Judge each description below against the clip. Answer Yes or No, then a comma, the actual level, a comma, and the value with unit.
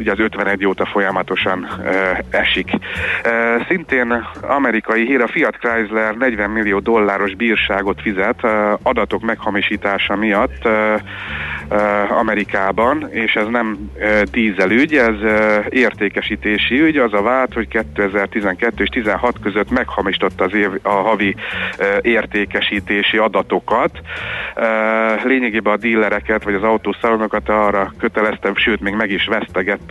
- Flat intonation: Yes, narrow, 1.8 semitones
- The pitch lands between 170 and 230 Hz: No, low, 105 Hz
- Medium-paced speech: Yes, average, 130 wpm